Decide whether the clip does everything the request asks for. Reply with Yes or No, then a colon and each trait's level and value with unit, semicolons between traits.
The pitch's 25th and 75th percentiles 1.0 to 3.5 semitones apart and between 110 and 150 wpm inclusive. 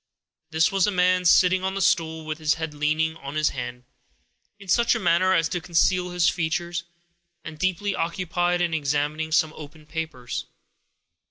No: average, 2.7 semitones; average, 170 wpm